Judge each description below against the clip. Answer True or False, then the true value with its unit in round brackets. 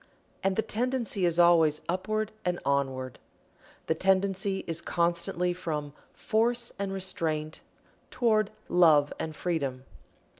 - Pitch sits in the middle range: True (175 Hz)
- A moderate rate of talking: False (115 wpm)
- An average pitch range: True (4.0 semitones)